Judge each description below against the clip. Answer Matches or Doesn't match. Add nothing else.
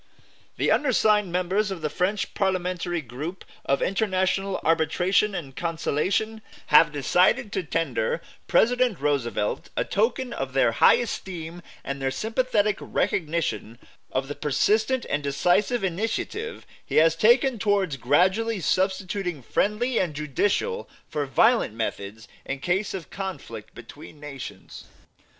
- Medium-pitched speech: Matches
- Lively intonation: Matches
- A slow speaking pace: Matches